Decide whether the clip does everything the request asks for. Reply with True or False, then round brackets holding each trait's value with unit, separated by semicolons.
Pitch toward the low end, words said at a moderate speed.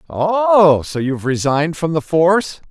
False (165 Hz; 155 wpm)